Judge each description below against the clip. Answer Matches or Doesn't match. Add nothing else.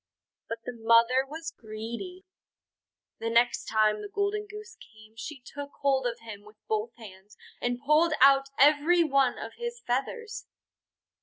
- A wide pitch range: Matches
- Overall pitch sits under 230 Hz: Doesn't match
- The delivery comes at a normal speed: Matches